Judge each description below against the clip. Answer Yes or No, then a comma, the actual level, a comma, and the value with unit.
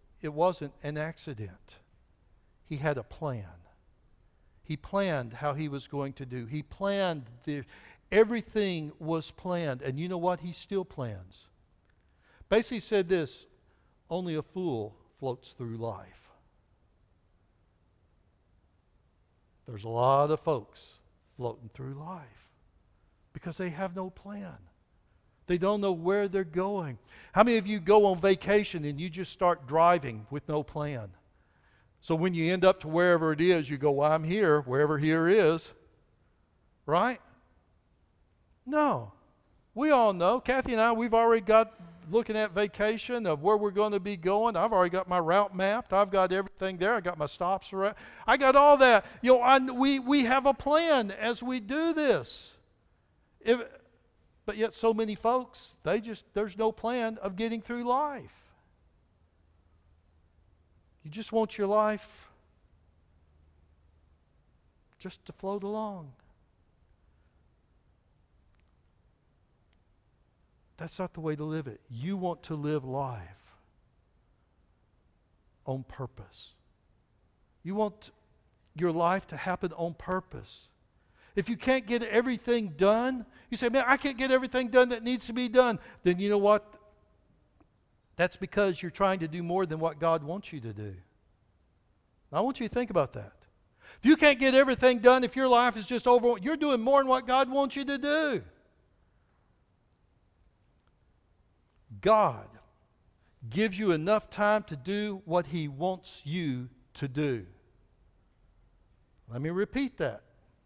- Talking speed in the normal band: Yes, average, 145 wpm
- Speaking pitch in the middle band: Yes, medium, 170 Hz